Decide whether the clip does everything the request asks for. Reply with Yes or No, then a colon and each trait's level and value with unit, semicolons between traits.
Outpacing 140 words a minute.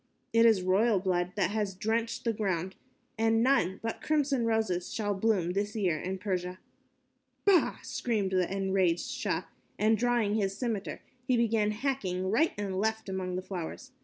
Yes: average, 160 wpm